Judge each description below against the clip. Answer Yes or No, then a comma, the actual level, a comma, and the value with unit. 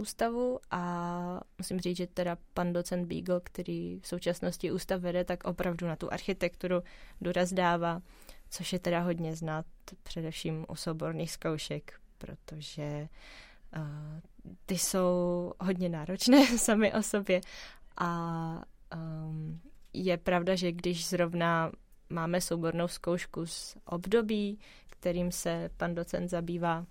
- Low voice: No, medium, 175 Hz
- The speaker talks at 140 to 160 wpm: No, average, 125 wpm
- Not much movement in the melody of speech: Yes, narrow, 1.6 semitones